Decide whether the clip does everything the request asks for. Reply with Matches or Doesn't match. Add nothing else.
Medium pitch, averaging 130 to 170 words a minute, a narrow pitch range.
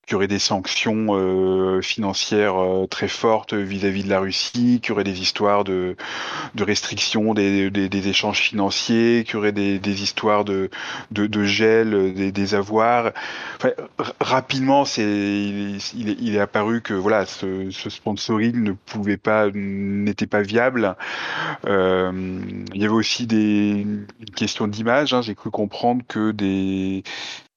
Doesn't match